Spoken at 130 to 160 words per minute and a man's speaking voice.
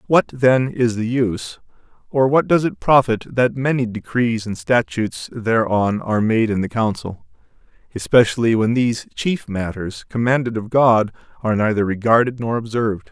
Yes: average, 155 wpm; male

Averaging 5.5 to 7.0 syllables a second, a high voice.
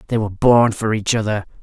No: 6.2 syllables/s; low, 110 Hz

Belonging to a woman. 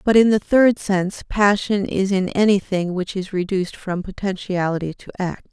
Yes: female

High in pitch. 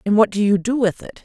Yes: high, 210 Hz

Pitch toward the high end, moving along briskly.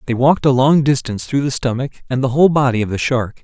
No: low, 130 Hz; fast, 260 wpm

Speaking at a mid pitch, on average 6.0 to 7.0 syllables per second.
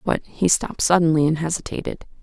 Yes: medium, 160 Hz; 6.1 syllables/s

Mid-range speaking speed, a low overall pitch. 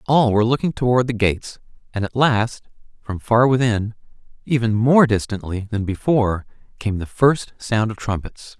Yes: average, 160 wpm; low, 115 Hz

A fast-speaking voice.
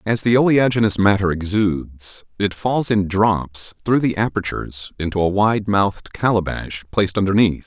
No: average, 150 wpm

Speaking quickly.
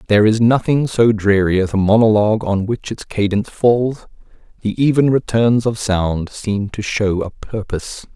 No: average, 170 wpm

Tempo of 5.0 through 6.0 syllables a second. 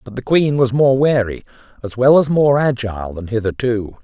Yes: 5.1 syllables/s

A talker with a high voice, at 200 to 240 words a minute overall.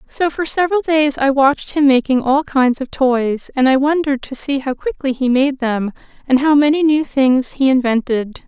Yes: very high, 270 Hz; fast, 205 wpm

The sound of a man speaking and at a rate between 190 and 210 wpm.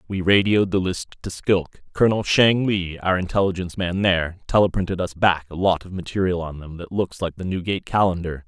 Yes: male; average, 200 wpm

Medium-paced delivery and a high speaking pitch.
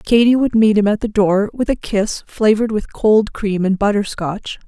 No: fast, 220 wpm; high, 210 Hz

